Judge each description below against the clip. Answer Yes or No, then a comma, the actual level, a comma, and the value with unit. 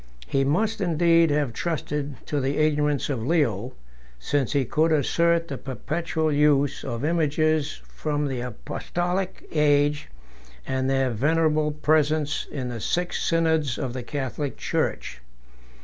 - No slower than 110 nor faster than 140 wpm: Yes, slow, 135 wpm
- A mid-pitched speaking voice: Yes, medium, 150 Hz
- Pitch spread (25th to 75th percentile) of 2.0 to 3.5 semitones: Yes, average, 2.9 semitones